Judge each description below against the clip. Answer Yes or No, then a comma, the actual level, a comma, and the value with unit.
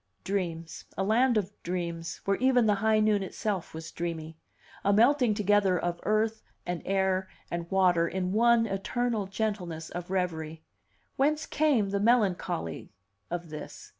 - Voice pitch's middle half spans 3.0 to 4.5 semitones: Yes, average, 4.0 semitones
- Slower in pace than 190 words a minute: Yes, average, 145 wpm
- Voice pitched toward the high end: Yes, high, 195 Hz